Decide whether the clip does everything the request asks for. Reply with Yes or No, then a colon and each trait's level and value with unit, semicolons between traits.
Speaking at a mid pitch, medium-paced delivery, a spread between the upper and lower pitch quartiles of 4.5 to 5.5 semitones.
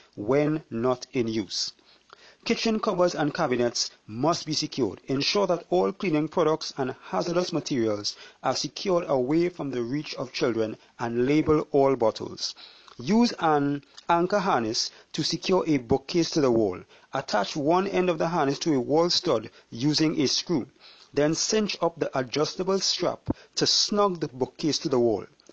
Yes: medium, 150 Hz; average, 160 wpm; average, 5.0 semitones